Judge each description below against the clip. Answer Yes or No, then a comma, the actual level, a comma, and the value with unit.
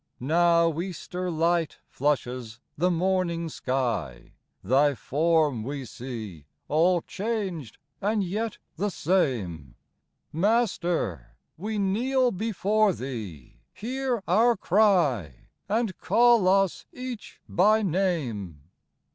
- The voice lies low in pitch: No, medium, 170 Hz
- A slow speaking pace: Yes, slow, 100 wpm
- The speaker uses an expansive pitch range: Yes, wide, 8.0 semitones